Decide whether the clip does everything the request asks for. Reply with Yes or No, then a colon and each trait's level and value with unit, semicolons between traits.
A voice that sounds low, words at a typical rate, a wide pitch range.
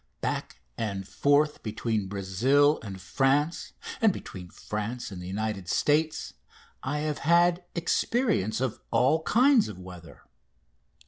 No: low, 125 Hz; slow, 125 wpm; wide, 7.8 semitones